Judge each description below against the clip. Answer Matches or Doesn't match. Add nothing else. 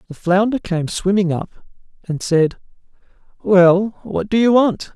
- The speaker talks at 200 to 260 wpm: Doesn't match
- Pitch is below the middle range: Doesn't match